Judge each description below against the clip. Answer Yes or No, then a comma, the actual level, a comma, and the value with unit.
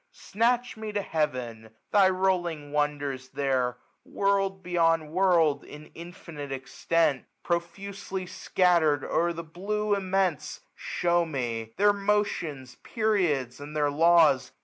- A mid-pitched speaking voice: Yes, medium, 170 Hz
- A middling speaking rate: No, slow, 115 wpm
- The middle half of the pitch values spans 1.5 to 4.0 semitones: No, average, 4.9 semitones